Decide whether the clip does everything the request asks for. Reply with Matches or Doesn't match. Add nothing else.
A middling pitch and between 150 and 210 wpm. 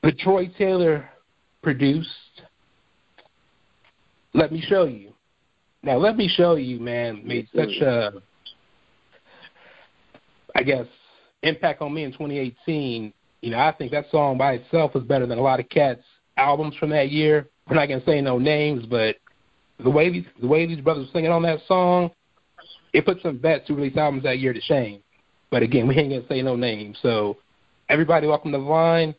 Matches